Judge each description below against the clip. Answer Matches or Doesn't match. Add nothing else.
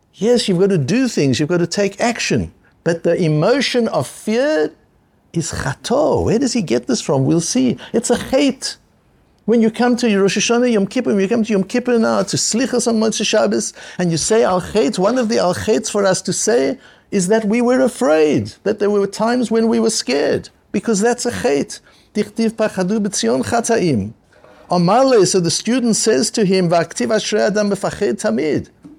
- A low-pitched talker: Doesn't match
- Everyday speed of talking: Matches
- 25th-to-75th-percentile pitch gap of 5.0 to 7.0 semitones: Doesn't match